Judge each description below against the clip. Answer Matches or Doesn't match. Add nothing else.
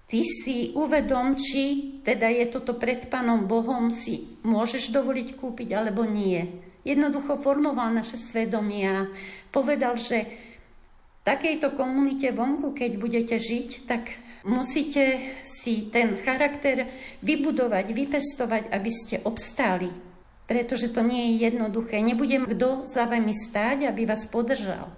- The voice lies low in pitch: Doesn't match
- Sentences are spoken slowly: Doesn't match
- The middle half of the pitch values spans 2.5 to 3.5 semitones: Matches